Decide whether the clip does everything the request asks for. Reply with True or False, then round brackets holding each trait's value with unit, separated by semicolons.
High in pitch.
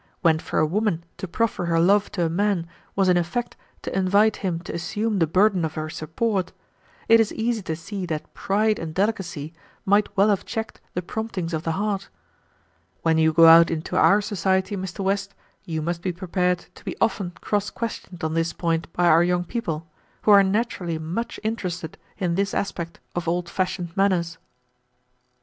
False (180 Hz)